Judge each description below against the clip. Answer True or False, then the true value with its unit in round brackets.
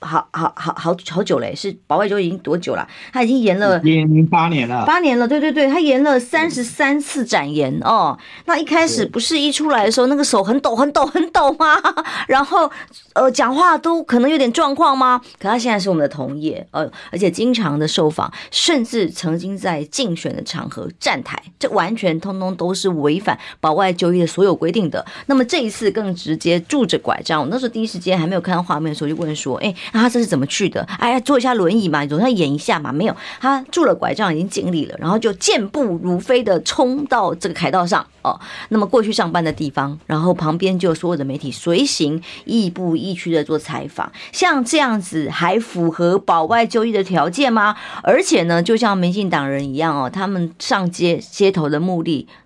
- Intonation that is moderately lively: False (7.1 semitones)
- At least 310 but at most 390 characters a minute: True (315 characters per minute)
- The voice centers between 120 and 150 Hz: False (195 Hz)